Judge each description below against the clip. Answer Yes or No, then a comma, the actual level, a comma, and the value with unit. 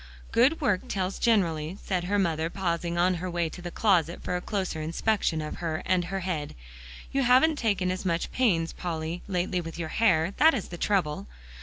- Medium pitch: Yes, medium, 180 Hz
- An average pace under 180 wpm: No, average, 195 wpm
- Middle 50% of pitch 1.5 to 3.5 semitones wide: Yes, average, 3.1 semitones